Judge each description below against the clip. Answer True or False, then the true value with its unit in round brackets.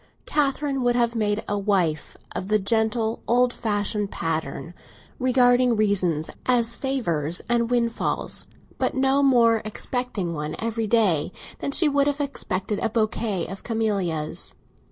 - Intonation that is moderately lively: True (4.1 semitones)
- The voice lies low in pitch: False (225 Hz)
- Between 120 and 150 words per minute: True (135 wpm)